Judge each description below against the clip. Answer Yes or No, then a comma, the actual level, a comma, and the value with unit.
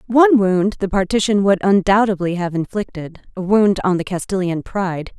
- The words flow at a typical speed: Yes, average, 160 wpm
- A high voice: Yes, high, 195 Hz